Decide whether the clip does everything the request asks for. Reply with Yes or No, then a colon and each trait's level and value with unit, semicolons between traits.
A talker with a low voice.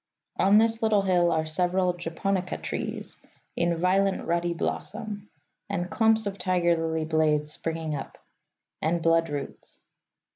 No: medium, 175 Hz